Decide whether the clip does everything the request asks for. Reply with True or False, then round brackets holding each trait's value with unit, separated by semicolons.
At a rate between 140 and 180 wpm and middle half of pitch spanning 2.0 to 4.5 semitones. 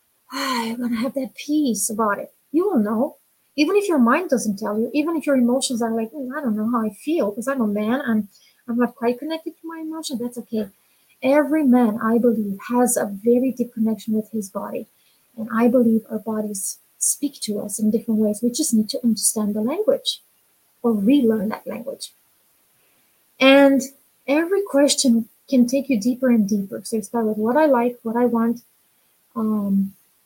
False (195 wpm; 3.8 semitones)